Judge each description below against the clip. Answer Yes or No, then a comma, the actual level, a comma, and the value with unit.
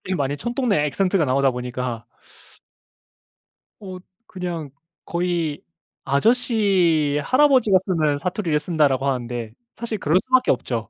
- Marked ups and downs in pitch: Yes, wide, 6.2 semitones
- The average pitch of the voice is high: No, medium, 165 Hz